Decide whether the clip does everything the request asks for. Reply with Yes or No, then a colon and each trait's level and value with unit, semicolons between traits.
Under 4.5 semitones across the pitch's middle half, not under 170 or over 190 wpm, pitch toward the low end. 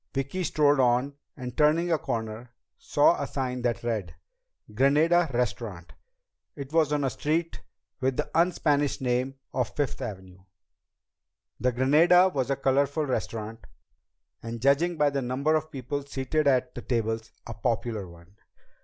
No: average, 3.9 semitones; average, 150 wpm; low, 130 Hz